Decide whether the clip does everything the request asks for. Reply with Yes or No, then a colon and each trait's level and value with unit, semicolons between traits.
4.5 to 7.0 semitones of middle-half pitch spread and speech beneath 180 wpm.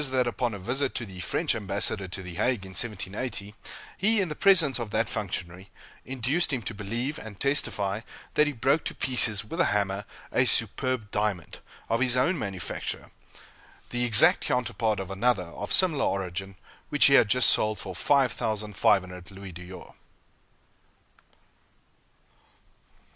Yes: average, 4.9 semitones; average, 150 wpm